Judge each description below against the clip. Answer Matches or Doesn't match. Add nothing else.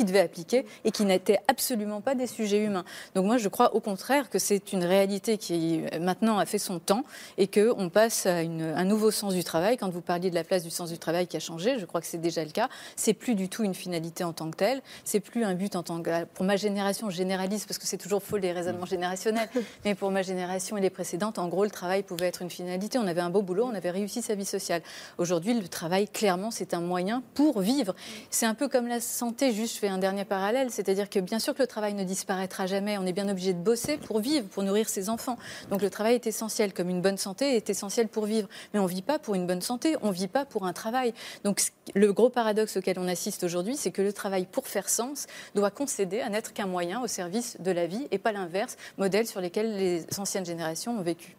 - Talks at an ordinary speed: Doesn't match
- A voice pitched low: Doesn't match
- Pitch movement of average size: Matches